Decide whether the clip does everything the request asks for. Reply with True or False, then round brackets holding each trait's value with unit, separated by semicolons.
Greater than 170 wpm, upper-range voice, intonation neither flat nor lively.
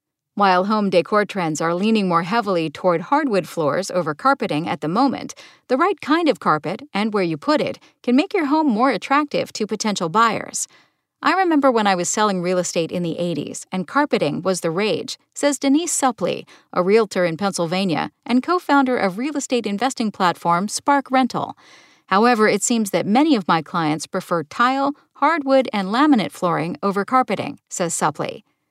False (180 wpm; 215 Hz; 7.2 semitones)